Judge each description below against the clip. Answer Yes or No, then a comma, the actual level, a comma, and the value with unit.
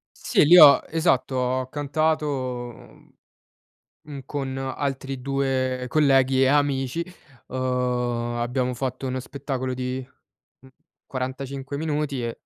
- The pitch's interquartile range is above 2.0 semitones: No, narrow, 1.7 semitones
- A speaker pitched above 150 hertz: No, low, 130 Hz